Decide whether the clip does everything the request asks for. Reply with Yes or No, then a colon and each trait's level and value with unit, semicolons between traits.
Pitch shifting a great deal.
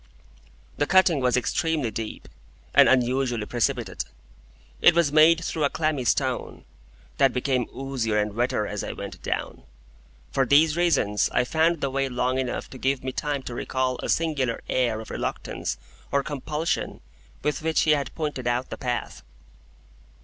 No: average, 3.6 semitones